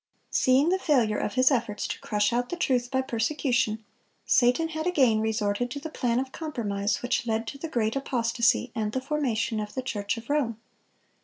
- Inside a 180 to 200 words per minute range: Yes, average, 190 wpm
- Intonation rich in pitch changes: No, average, 3.8 semitones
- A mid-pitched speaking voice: No, high, 245 Hz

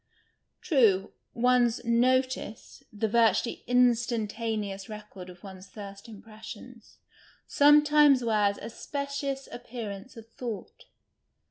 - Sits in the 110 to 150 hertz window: No, high, 230 Hz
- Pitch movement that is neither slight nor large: Yes, average, 3.2 semitones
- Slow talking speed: Yes, slow, 120 wpm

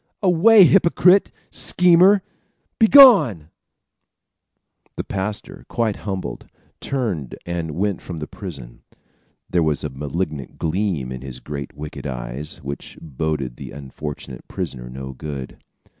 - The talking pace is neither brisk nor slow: No, slow, 115 wpm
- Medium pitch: No, very low, 80 Hz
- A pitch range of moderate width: No, wide, 8.1 semitones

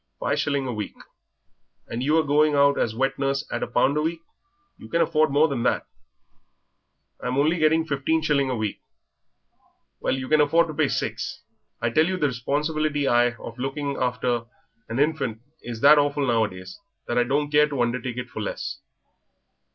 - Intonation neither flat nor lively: Yes, average, 3.7 semitones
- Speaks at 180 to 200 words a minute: Yes, average, 185 wpm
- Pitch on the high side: No, medium, 140 Hz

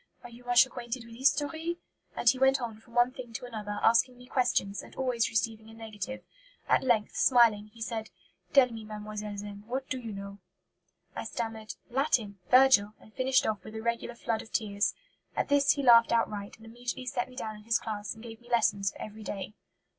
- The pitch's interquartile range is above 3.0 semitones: No, average, 2.7 semitones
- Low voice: No, high, 230 Hz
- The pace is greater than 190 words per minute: Yes, fast, 205 wpm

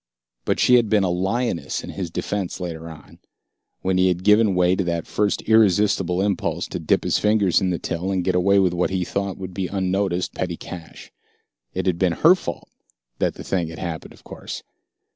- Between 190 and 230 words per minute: Yes, fast, 205 wpm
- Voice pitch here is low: Yes, very low, 95 Hz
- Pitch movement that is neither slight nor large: No, narrow, 2.1 semitones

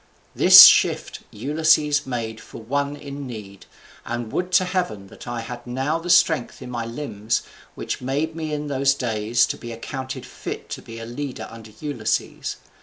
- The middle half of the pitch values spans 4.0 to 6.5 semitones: Yes, average, 4.3 semitones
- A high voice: No, low, 130 Hz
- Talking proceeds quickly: No, average, 175 wpm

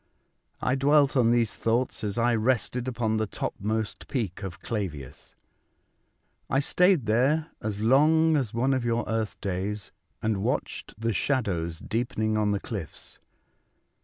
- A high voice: No, low, 115 Hz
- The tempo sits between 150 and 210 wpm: No, average, 140 wpm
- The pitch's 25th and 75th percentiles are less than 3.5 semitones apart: No, average, 3.8 semitones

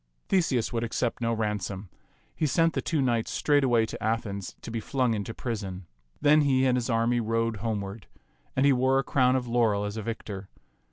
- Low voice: Yes, low, 115 Hz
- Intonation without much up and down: No, average, 3.2 semitones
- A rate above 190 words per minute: Yes, average, 200 wpm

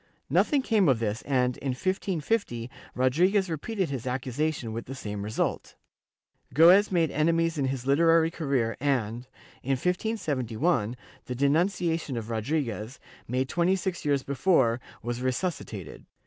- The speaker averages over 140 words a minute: No, slow, 135 wpm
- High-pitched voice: No, medium, 140 Hz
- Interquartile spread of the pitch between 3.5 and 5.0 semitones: No, wide, 5.5 semitones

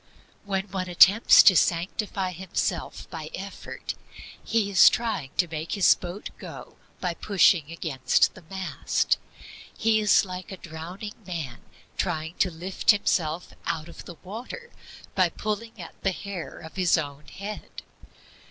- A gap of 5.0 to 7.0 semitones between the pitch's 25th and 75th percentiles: No, average, 3.2 semitones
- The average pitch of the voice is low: No, medium, 185 Hz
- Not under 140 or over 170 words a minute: Yes, average, 145 wpm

